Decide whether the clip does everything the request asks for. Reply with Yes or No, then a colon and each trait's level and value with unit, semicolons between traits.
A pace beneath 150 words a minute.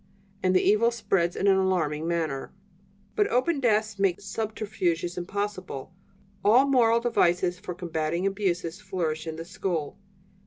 Yes: average, 140 wpm